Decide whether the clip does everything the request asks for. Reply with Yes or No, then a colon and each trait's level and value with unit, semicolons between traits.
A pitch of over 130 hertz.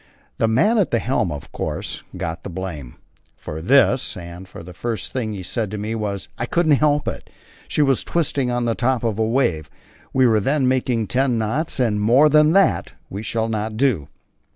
No: low, 115 Hz